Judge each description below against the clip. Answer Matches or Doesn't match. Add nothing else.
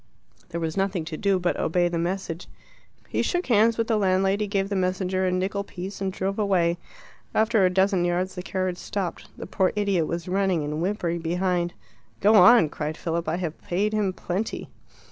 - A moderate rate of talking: Matches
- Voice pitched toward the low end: Doesn't match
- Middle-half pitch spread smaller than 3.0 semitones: Matches